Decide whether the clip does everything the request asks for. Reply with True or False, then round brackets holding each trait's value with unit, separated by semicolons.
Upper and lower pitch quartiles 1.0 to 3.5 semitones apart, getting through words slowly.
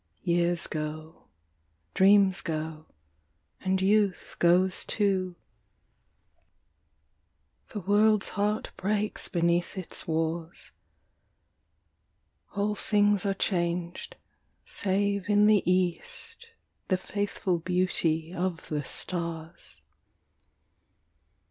True (3.1 semitones; 80 wpm)